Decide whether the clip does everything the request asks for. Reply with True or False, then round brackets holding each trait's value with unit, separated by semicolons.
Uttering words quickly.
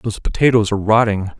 False (170 wpm)